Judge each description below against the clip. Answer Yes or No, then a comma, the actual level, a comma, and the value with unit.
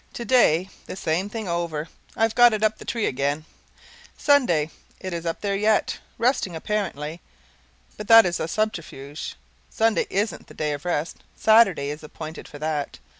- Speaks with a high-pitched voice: No, medium, 175 Hz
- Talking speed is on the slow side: No, average, 165 wpm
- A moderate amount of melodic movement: No, wide, 5.8 semitones